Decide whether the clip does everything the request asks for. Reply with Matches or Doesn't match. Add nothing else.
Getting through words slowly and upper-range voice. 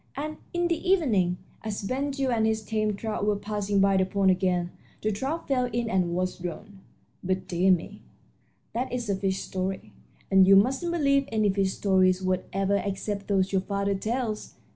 Doesn't match